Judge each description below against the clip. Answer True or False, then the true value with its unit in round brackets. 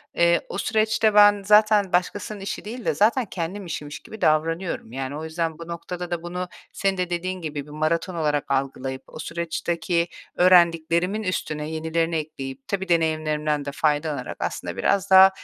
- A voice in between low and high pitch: True (170 Hz)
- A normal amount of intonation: True (3.5 semitones)